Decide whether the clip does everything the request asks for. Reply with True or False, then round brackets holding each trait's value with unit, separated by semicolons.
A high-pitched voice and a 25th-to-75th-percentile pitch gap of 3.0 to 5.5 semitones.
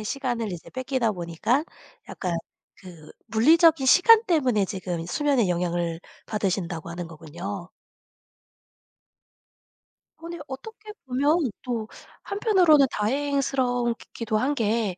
False (235 Hz; 7.7 semitones)